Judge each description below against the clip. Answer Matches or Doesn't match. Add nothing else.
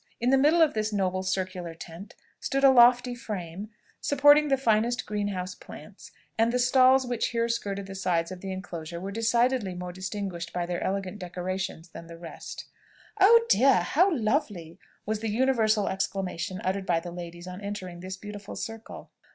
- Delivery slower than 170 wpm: Doesn't match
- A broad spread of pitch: Doesn't match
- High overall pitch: Matches